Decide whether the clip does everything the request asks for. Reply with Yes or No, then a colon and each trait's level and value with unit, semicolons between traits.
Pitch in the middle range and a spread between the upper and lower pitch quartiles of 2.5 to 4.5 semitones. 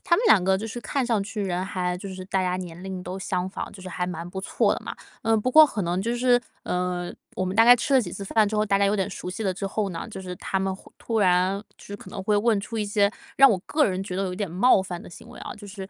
No: high, 195 Hz; average, 3.0 semitones